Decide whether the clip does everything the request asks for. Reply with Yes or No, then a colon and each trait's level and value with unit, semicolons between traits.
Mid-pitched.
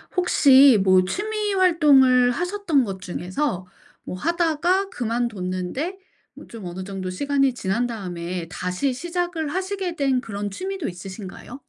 No: very high, 255 Hz